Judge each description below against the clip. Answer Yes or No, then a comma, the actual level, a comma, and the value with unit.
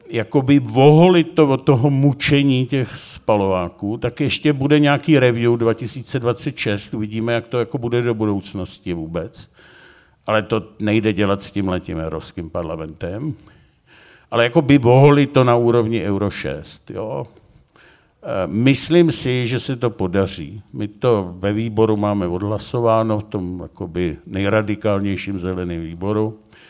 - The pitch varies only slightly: No, average, 4.8 semitones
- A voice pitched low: Yes, low, 110 Hz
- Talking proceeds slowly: No, average, 125 wpm